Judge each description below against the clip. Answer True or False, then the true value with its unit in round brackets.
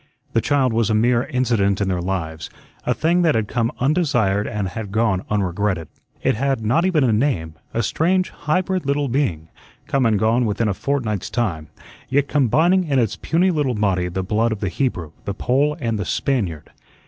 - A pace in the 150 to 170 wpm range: False (190 wpm)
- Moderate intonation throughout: False (6.0 semitones)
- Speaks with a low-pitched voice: True (115 Hz)